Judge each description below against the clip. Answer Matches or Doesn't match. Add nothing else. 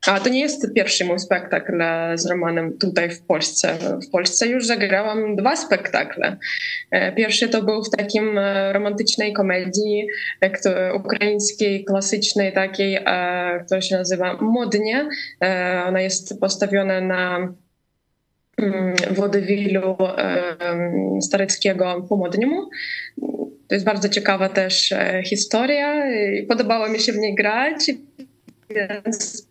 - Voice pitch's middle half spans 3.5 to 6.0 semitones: Doesn't match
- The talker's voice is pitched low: Doesn't match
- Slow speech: Matches